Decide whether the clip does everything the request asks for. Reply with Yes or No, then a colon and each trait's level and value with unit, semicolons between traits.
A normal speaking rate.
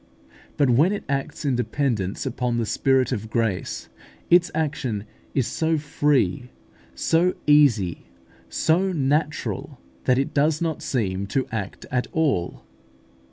No: slow, 130 wpm